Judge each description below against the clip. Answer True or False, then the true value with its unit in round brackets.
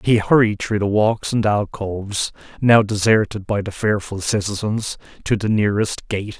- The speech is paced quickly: False (170 wpm)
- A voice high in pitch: False (105 Hz)